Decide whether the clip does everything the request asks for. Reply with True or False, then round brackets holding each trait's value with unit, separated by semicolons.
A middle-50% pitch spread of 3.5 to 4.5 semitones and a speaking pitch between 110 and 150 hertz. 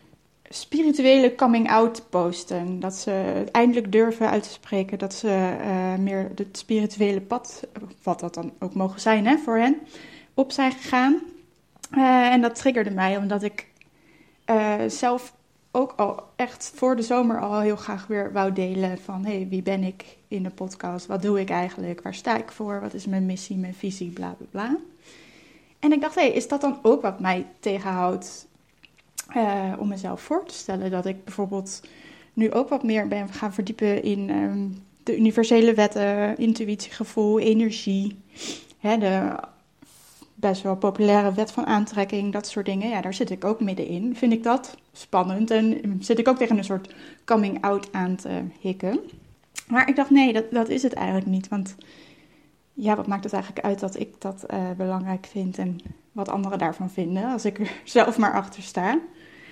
False (3.8 semitones; 210 Hz)